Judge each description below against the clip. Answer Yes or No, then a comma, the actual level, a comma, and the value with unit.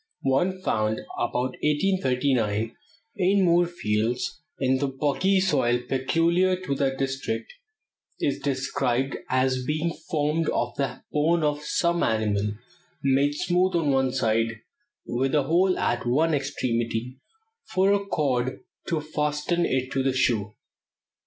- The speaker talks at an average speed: No, slow, 125 wpm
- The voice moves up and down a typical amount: Yes, average, 4.7 semitones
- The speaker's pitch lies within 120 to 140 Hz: Yes, low, 135 Hz